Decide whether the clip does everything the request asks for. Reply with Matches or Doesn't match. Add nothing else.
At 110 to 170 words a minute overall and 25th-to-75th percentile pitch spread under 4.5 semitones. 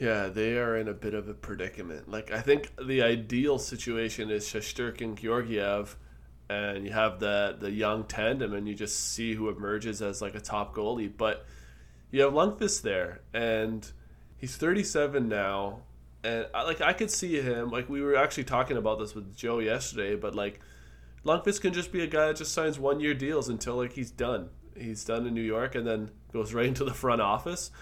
Doesn't match